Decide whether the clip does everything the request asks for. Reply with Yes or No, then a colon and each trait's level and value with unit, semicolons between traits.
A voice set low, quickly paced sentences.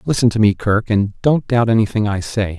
Yes: low, 110 Hz; fast, 210 wpm